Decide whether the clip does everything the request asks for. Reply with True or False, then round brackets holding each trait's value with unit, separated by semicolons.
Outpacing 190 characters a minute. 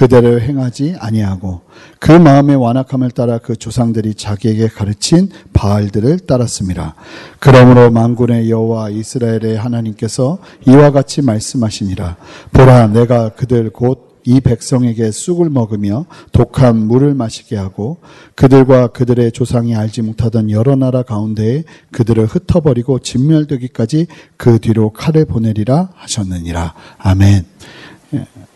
True (315 characters per minute)